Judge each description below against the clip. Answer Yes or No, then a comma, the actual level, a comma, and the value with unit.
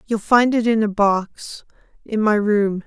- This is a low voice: No, high, 215 Hz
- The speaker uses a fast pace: No, average, 170 wpm